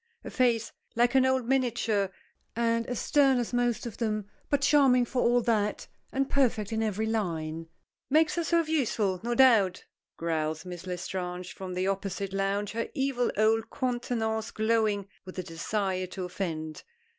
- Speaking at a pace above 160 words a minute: No, average, 155 wpm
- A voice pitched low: No, high, 220 Hz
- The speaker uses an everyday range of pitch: Yes, average, 4.5 semitones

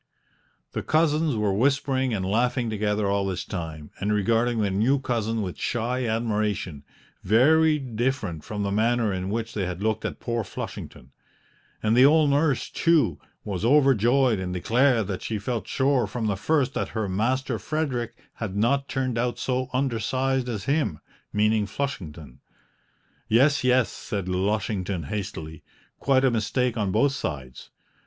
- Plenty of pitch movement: No, average, 4.6 semitones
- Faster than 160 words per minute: No, average, 155 wpm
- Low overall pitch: Yes, low, 115 Hz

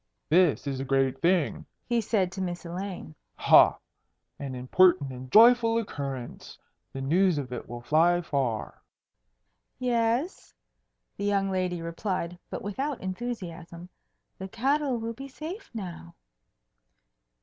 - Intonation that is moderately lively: No, wide, 7.7 semitones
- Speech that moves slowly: Yes, slow, 125 wpm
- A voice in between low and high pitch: Yes, medium, 180 Hz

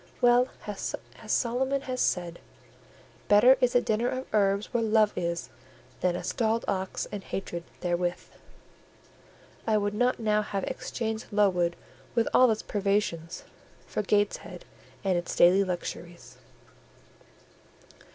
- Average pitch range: Yes, average, 4.2 semitones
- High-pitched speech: Yes, high, 205 Hz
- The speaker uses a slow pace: Yes, slow, 120 wpm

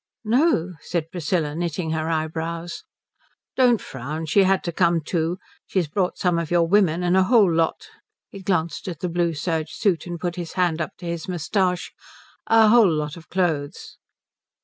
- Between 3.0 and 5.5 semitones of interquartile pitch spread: No, narrow, 2.5 semitones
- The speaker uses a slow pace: No, average, 175 wpm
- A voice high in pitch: No, medium, 170 Hz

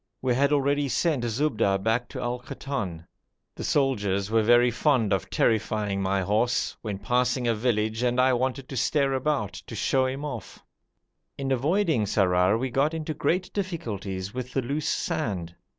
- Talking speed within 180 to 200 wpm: No, average, 165 wpm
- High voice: No, low, 120 Hz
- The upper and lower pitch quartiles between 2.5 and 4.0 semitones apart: No, average, 4.7 semitones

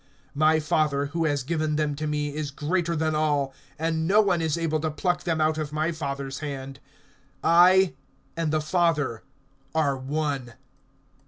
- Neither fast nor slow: Yes, average, 165 wpm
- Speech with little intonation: Yes, narrow, 2.2 semitones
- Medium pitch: Yes, medium, 155 Hz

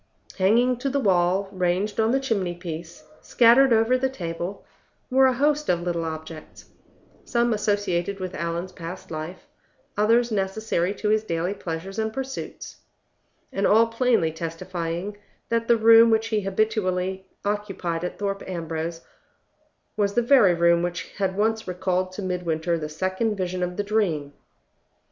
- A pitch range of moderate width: Yes, average, 4.3 semitones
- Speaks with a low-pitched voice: No, high, 190 Hz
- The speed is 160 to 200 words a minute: No, average, 150 wpm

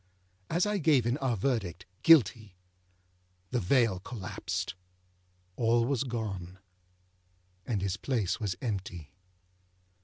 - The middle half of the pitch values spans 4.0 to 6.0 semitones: Yes, average, 5.1 semitones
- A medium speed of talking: No, slow, 110 wpm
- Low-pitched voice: Yes, low, 115 Hz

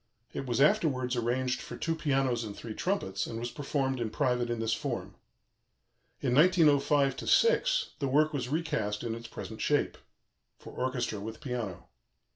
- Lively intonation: No, average, 3.9 semitones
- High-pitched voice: No, low, 130 Hz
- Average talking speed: Yes, average, 160 wpm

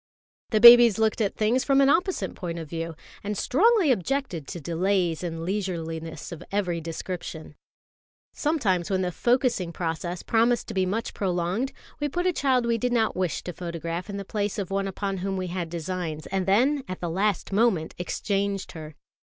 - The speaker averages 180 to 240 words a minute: Yes, average, 185 wpm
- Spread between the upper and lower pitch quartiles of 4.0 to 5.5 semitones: Yes, average, 5.1 semitones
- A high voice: Yes, high, 195 Hz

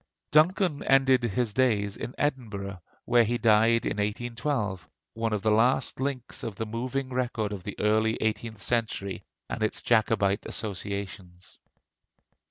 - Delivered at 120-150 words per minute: Yes, average, 140 wpm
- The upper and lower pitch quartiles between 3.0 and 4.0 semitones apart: Yes, average, 3.4 semitones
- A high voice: No, low, 110 Hz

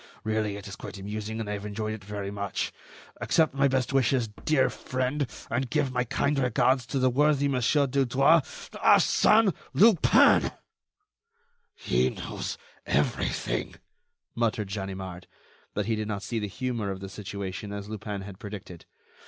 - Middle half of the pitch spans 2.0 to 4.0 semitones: No, average, 4.6 semitones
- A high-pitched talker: No, low, 110 Hz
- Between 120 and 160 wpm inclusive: Yes, average, 155 wpm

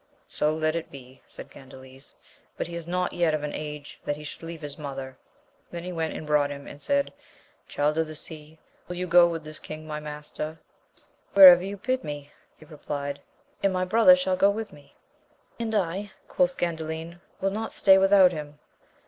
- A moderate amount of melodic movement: Yes, average, 3.5 semitones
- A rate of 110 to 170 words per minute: No, average, 195 wpm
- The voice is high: No, medium, 160 Hz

